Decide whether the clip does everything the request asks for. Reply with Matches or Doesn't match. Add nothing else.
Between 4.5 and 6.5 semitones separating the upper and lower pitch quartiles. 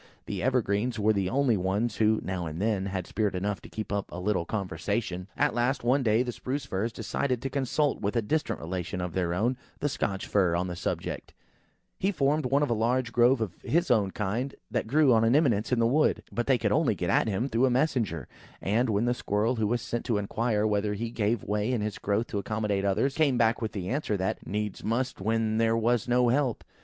Doesn't match